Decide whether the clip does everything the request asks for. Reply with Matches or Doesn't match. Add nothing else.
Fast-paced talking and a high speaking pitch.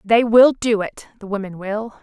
Doesn't match